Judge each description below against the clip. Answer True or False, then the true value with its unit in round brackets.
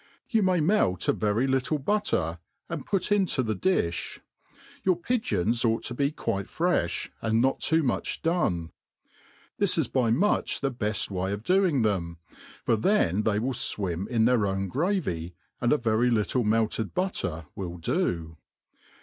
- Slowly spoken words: False (160 wpm)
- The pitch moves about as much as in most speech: False (8.7 semitones)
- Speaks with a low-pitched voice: True (115 Hz)